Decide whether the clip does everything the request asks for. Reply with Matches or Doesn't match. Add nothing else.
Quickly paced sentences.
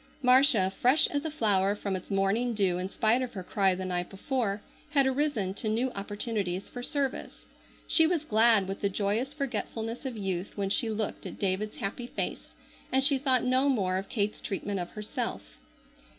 Doesn't match